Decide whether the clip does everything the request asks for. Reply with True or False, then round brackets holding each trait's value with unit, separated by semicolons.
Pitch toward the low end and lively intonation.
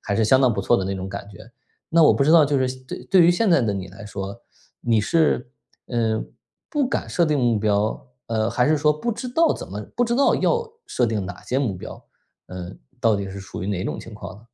True (115 Hz; 7.3 semitones)